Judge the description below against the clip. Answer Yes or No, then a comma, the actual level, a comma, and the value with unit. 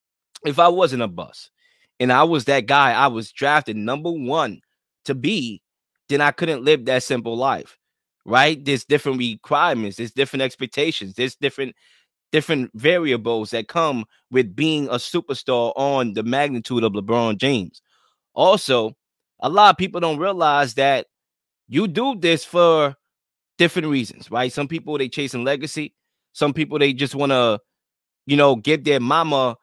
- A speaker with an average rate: Yes, average, 160 wpm